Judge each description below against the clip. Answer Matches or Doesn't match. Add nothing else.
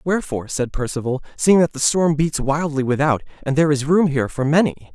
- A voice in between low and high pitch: Matches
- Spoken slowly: Doesn't match